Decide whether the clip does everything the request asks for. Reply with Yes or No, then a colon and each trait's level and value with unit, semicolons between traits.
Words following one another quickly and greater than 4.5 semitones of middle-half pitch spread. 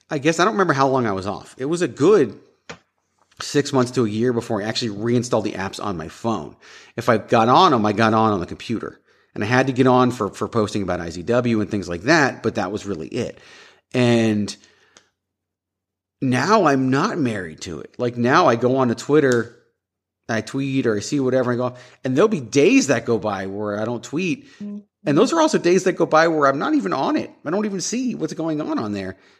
Yes: fast, 235 wpm; average, 5.0 semitones